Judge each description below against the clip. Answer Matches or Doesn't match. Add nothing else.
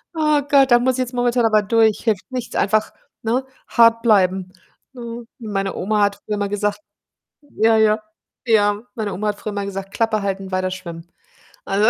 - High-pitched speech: Matches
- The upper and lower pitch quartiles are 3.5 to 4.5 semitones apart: Doesn't match